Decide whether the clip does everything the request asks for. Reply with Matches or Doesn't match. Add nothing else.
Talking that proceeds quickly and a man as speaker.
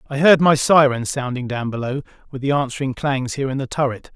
Matches